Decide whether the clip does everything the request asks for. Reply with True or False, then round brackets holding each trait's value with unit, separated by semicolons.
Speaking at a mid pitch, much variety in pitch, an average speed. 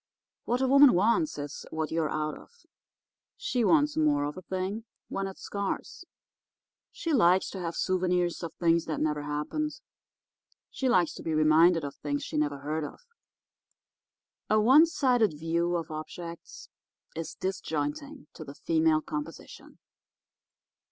True (170 Hz; 5.9 semitones; 145 wpm)